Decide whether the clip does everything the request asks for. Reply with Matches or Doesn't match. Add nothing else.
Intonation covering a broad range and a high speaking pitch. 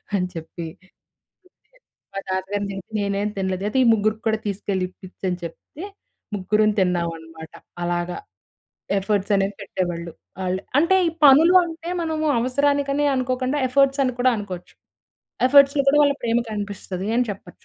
Matches